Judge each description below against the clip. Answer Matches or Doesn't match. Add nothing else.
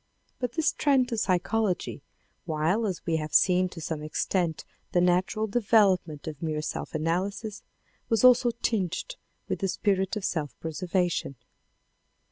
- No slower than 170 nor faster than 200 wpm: Doesn't match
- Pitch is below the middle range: Doesn't match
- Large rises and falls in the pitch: Doesn't match